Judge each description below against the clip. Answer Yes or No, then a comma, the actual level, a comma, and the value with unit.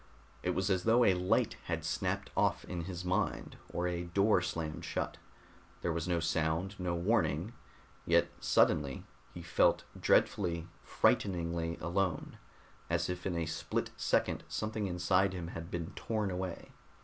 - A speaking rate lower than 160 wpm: Yes, average, 150 wpm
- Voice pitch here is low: Yes, very low, 90 Hz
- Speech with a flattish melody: Yes, narrow, 2.0 semitones